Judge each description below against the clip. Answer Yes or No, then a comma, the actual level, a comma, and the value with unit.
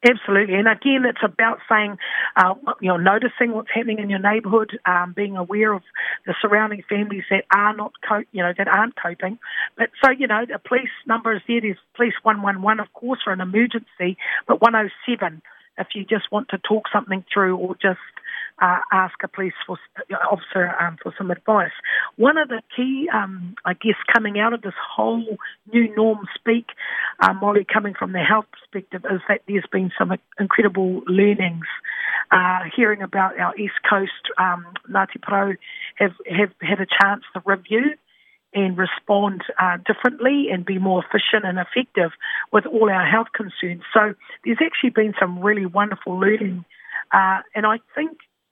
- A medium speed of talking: Yes, average, 175 wpm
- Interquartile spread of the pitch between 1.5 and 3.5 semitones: Yes, average, 2.9 semitones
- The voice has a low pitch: No, high, 205 Hz